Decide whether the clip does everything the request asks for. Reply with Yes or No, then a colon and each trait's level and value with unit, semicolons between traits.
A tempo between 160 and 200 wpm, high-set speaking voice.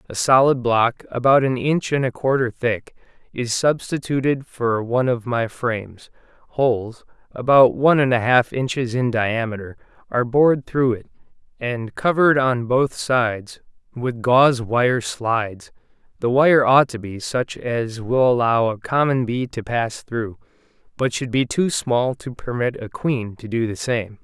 No: average, 165 wpm; low, 125 Hz